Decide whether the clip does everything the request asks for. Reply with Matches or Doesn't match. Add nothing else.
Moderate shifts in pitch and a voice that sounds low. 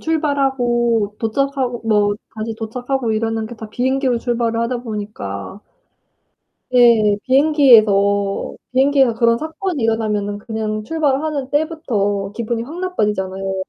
Doesn't match